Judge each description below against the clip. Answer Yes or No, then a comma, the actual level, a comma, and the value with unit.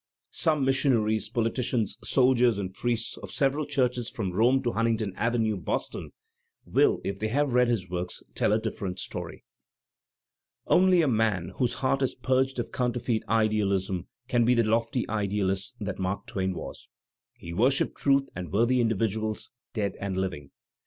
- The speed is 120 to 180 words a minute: Yes, average, 160 wpm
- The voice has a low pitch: Yes, low, 115 Hz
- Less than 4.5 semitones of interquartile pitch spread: Yes, average, 4.0 semitones